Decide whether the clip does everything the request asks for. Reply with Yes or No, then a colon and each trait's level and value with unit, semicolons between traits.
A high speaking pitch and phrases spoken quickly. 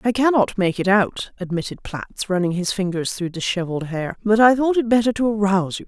Yes: high, 200 Hz; fast, 215 wpm